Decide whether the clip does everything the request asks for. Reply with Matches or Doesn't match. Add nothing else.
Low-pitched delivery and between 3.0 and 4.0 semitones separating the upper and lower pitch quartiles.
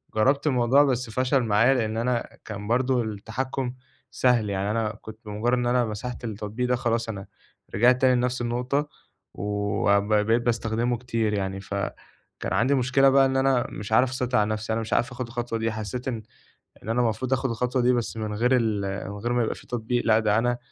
Doesn't match